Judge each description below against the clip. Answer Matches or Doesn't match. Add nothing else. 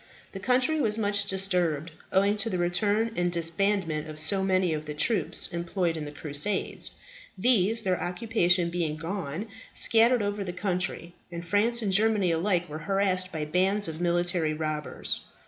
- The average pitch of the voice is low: Doesn't match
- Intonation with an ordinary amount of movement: Matches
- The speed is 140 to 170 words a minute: Matches